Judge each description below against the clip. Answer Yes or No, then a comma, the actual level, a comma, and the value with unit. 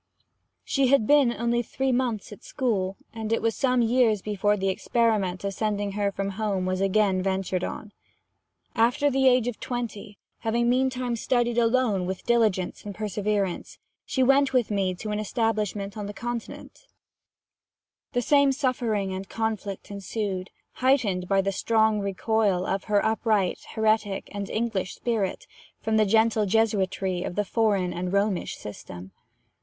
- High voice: Yes, high, 215 Hz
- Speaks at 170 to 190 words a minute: No, average, 155 wpm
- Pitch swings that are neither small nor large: Yes, average, 3.3 semitones